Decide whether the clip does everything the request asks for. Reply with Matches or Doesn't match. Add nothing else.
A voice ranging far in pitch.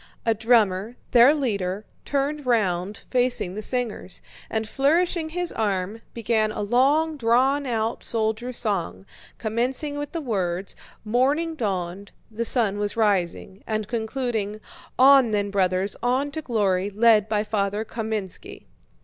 Doesn't match